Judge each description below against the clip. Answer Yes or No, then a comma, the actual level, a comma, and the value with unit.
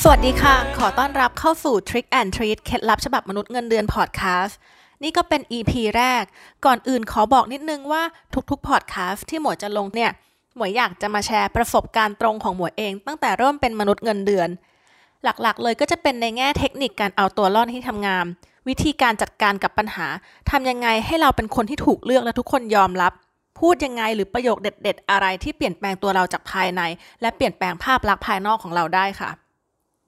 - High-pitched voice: Yes, high, 230 Hz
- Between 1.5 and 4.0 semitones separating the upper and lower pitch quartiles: No, average, 4.7 semitones